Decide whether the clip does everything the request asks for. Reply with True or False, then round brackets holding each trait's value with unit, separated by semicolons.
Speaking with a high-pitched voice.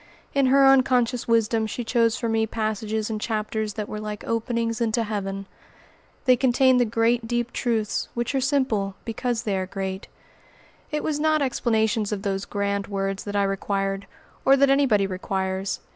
True (220 Hz)